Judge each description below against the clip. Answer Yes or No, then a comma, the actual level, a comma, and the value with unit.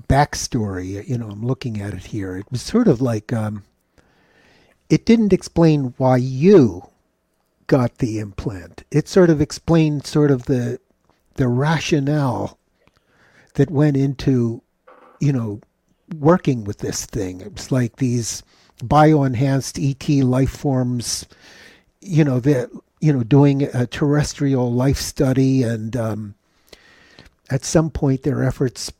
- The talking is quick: No, slow, 135 wpm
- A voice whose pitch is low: Yes, low, 130 Hz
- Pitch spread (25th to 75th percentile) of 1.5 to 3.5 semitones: No, average, 4.1 semitones